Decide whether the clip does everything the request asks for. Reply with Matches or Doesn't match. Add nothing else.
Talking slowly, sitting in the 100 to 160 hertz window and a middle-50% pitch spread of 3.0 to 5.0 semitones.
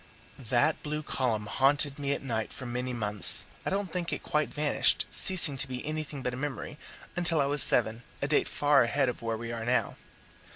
Doesn't match